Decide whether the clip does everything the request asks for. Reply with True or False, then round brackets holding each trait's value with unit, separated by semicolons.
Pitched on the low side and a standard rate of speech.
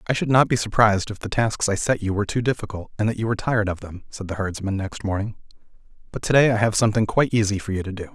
False (105 Hz; 280 wpm)